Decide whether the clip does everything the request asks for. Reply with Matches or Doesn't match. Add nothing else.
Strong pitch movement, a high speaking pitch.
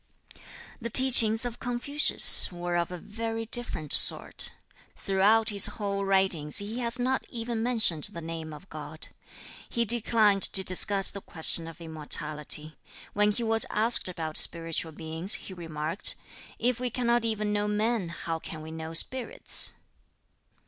Matches